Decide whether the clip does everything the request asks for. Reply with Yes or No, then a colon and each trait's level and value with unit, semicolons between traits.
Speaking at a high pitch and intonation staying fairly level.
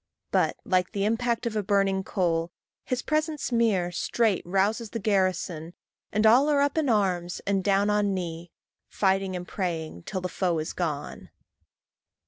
No: high, 195 Hz; average, 3.8 semitones